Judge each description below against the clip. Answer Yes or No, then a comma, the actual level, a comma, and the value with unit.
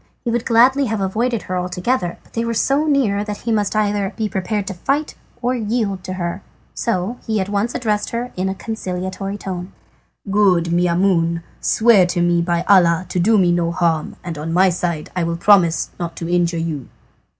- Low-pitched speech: No, high, 190 Hz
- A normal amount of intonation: Yes, average, 4.1 semitones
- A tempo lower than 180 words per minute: No, average, 195 wpm